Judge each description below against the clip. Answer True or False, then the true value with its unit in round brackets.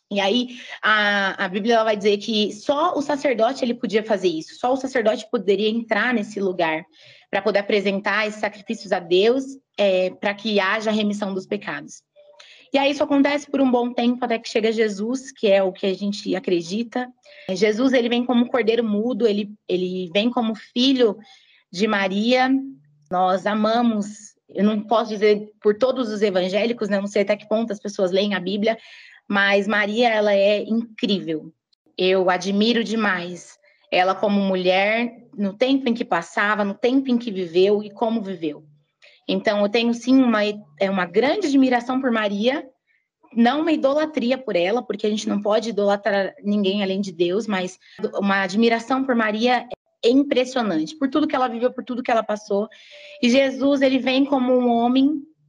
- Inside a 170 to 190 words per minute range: True (180 wpm)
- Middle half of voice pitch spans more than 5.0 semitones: False (3.8 semitones)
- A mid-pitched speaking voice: False (220 Hz)